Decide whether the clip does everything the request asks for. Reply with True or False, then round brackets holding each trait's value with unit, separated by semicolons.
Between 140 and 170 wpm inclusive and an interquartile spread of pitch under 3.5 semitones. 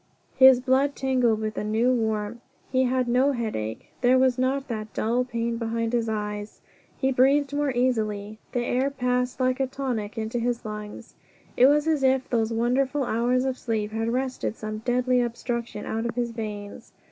False (180 wpm; 2.7 semitones)